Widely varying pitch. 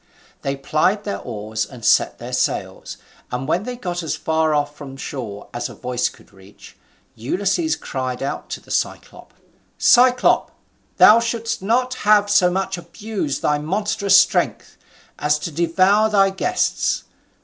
Yes: wide, 7.3 semitones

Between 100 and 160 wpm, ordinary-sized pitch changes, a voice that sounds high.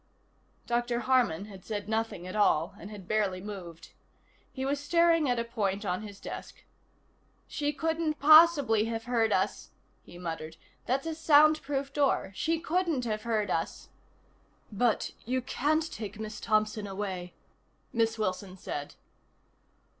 No: average, 140 wpm; wide, 5.9 semitones; high, 225 Hz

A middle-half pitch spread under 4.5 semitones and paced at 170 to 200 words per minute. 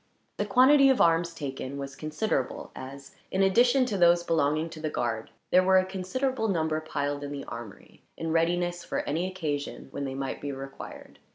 No: average, 4.9 semitones; average, 185 wpm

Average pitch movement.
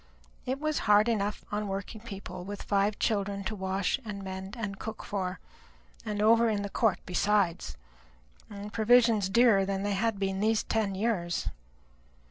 No: narrow, 2.2 semitones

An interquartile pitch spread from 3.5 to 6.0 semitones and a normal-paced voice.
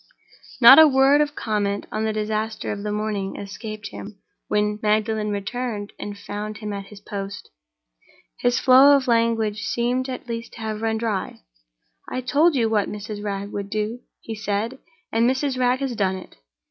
No: average, 2.9 semitones; average, 175 wpm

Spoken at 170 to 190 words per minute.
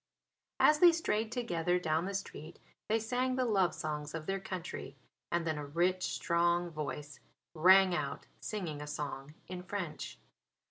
No: average, 155 wpm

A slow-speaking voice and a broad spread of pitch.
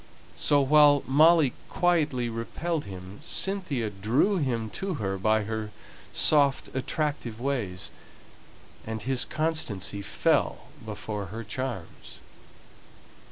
Yes: slow, 105 wpm; wide, 5.7 semitones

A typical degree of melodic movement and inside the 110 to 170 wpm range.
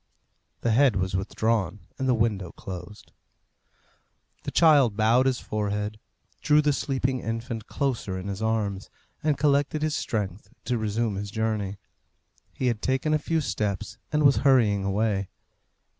Yes: average, 4.7 semitones; average, 145 wpm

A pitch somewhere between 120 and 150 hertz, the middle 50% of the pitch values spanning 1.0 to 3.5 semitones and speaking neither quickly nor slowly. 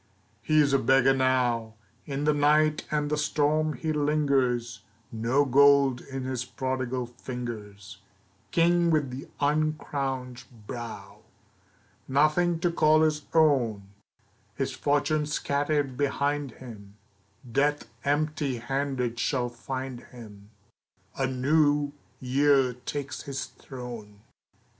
No: low, 135 Hz; average, 3.0 semitones; slow, 110 wpm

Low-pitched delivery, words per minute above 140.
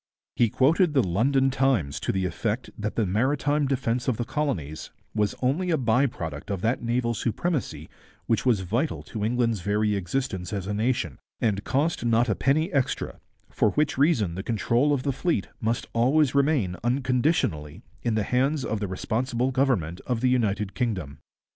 Yes: low, 120 Hz; average, 175 wpm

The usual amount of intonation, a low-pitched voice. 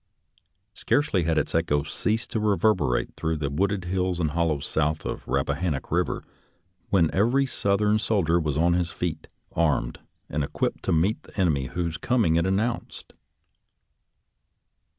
Yes: average, 4.3 semitones; very low, 85 Hz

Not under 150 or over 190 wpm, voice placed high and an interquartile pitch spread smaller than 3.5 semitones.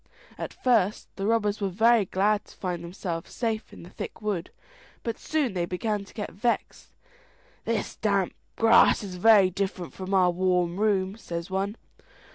Yes: average, 165 wpm; high, 200 Hz; average, 2.9 semitones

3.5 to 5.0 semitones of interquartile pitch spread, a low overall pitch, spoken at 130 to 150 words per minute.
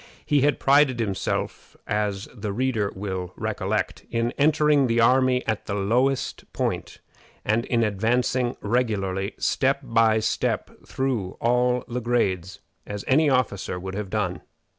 Yes: average, 4.1 semitones; low, 115 Hz; average, 140 wpm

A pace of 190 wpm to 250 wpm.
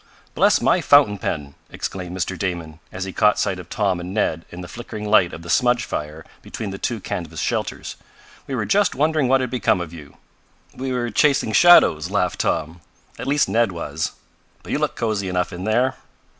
Yes: average, 200 wpm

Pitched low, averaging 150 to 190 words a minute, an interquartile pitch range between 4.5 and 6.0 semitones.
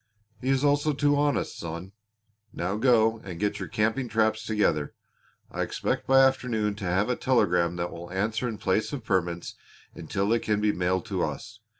Yes: low, 110 Hz; average, 185 wpm; average, 5.2 semitones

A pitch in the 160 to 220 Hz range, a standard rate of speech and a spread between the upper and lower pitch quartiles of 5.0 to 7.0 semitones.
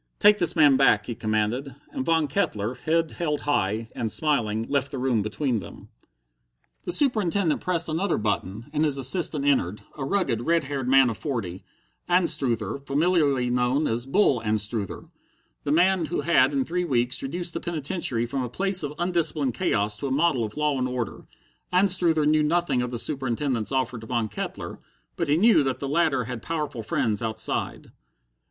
No: medium, 140 Hz; average, 175 wpm; wide, 5.6 semitones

